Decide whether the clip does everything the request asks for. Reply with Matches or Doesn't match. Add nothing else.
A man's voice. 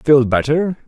Matches